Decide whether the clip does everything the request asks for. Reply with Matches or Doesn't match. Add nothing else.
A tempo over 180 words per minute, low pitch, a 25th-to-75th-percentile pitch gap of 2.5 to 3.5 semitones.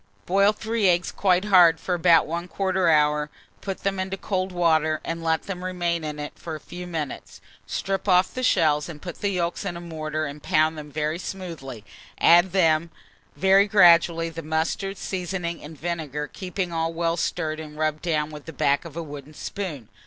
Doesn't match